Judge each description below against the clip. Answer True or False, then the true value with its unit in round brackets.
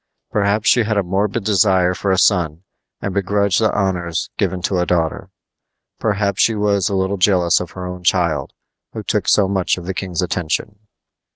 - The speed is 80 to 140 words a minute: False (185 wpm)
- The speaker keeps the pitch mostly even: True (2.2 semitones)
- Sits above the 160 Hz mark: False (95 Hz)